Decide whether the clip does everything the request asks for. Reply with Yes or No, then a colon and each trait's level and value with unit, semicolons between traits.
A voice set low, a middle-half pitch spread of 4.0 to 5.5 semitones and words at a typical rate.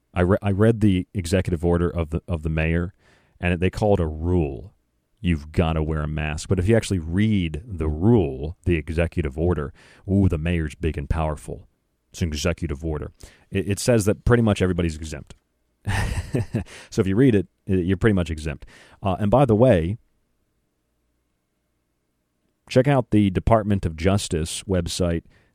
Yes: very low, 90 Hz; average, 4.3 semitones; average, 170 wpm